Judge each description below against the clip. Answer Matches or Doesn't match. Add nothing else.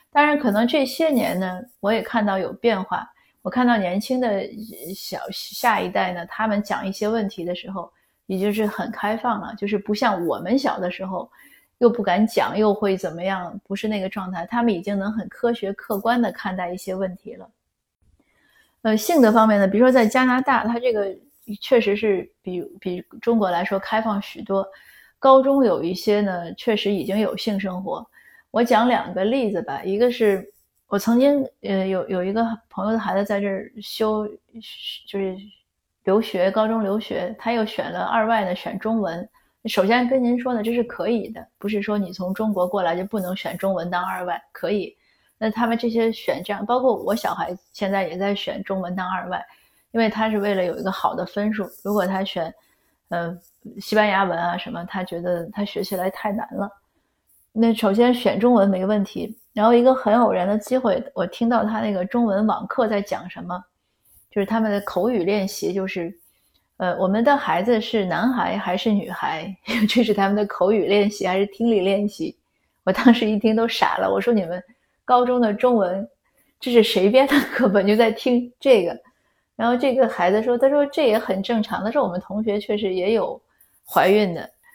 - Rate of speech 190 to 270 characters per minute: Doesn't match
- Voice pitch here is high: Matches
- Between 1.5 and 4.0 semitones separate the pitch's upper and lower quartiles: Matches